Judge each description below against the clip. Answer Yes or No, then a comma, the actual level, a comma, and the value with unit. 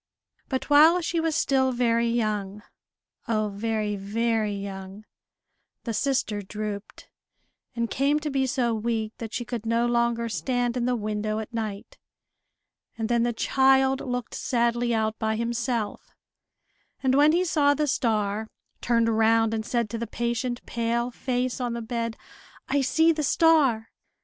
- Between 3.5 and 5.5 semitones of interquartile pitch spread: No, average, 2.8 semitones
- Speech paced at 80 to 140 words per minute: No, average, 155 wpm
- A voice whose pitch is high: Yes, high, 235 Hz